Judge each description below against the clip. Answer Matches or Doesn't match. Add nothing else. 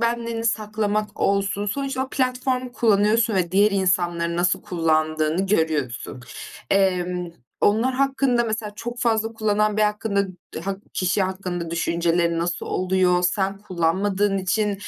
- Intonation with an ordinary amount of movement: Matches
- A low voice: Doesn't match